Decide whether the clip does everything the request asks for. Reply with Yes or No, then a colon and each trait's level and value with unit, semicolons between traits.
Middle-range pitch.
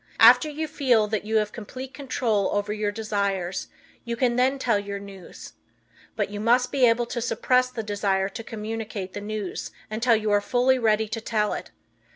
No: high, 220 Hz